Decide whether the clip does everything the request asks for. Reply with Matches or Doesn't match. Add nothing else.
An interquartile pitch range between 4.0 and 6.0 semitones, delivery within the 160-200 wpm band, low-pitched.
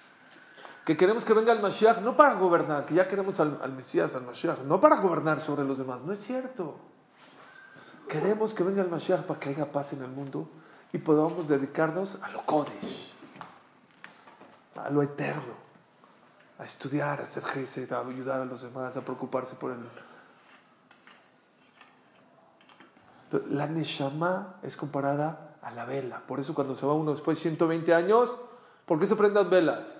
Doesn't match